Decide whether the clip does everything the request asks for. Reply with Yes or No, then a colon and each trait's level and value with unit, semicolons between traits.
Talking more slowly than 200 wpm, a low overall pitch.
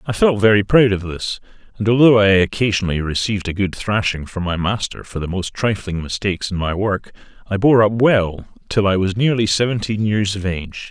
No: fast, 205 wpm; low, 100 Hz